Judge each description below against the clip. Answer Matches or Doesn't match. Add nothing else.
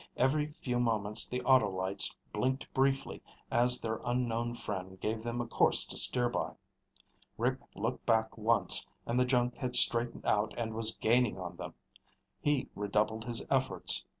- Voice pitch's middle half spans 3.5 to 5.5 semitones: Doesn't match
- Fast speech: Doesn't match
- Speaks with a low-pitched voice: Matches